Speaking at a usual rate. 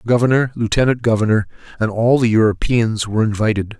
Yes: average, 160 wpm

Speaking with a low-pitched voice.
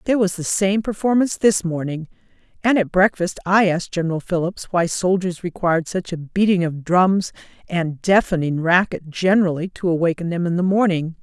No: medium, 180 Hz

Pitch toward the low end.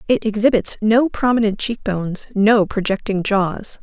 No: high, 210 Hz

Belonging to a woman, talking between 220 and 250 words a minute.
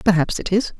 Yes: female; fast, 230 wpm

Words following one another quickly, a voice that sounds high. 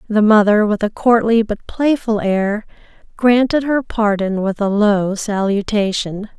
No: average, 140 wpm; high, 215 Hz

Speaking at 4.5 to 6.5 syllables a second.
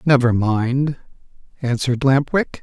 No: 4.0 syllables/s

